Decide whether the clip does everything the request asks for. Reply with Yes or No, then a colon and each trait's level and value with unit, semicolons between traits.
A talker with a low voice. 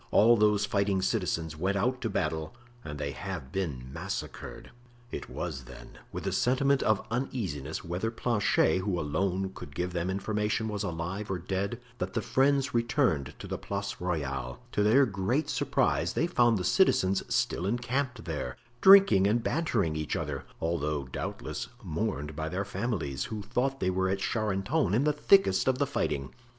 Yes: low, 100 Hz